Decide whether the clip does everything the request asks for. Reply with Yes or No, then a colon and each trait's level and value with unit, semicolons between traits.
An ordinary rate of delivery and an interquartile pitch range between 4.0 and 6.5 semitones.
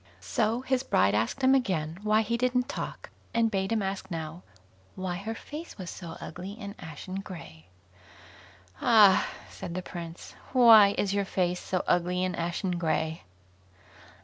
Yes: average, 155 wpm; average, 4.4 semitones